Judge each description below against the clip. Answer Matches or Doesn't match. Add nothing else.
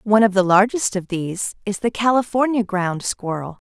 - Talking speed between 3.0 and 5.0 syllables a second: Doesn't match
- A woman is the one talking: Matches